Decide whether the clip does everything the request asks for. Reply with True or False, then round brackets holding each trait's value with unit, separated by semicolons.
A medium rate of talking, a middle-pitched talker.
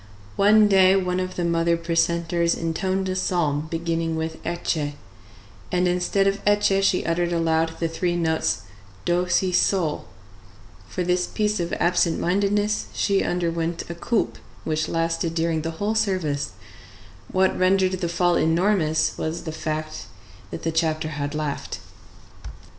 True (145 wpm; 170 Hz)